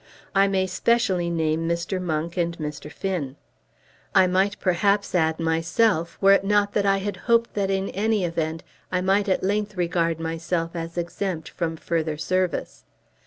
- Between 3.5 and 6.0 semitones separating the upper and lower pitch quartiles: No, average, 3.1 semitones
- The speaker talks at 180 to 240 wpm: No, average, 165 wpm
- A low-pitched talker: No, medium, 180 Hz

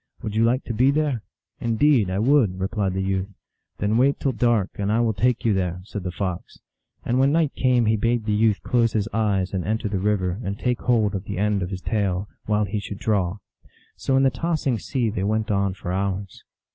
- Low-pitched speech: Yes, low, 105 Hz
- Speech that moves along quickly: Yes, fast, 235 wpm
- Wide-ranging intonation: No, average, 3.4 semitones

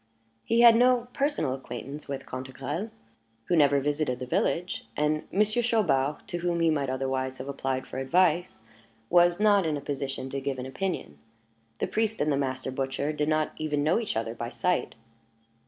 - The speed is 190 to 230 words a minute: No, average, 180 wpm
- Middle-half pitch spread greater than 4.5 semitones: Yes, average, 5.0 semitones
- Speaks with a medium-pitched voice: Yes, medium, 150 Hz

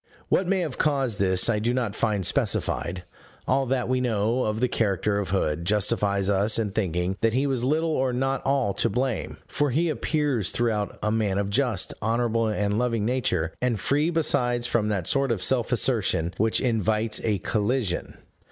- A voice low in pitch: Yes, low, 115 Hz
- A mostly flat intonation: No, average, 4.1 semitones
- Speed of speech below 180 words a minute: No, average, 190 wpm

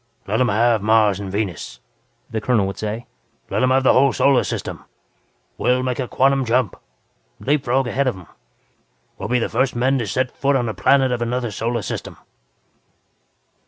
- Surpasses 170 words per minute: Yes, average, 190 wpm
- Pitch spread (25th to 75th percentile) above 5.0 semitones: No, average, 3.0 semitones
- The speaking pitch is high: No, low, 125 Hz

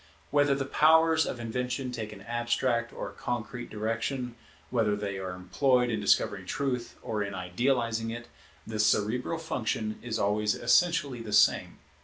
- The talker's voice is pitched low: Yes, low, 120 Hz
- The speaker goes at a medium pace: Yes, average, 155 wpm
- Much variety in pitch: No, average, 3.0 semitones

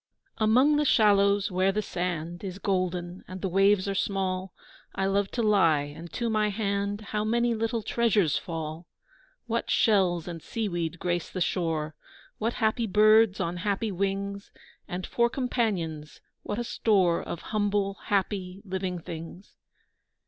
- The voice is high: Yes, high, 195 Hz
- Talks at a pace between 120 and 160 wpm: Yes, average, 150 wpm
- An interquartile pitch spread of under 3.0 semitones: No, average, 3.3 semitones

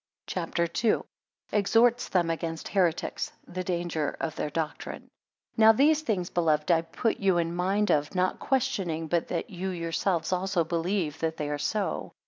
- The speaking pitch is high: No, medium, 175 Hz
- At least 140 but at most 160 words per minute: No, average, 170 wpm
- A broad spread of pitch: No, average, 3.2 semitones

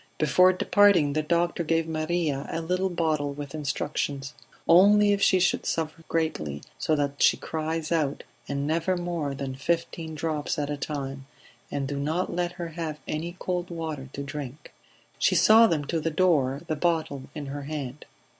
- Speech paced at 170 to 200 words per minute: Yes, average, 175 wpm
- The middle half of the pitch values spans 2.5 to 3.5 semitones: Yes, average, 3.2 semitones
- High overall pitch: No, medium, 155 Hz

